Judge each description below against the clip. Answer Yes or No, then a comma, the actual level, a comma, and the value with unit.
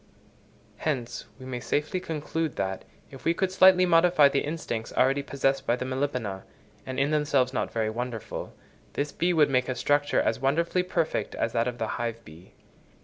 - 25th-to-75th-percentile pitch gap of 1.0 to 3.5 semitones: No, average, 4.3 semitones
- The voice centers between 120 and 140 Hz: Yes, low, 135 Hz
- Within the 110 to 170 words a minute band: No, average, 180 wpm